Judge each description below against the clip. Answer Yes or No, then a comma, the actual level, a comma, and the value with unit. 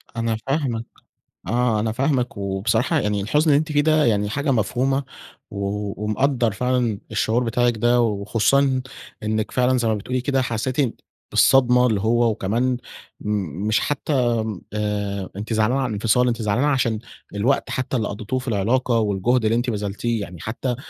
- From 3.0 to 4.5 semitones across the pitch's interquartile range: Yes, average, 3.4 semitones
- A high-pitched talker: No, low, 115 Hz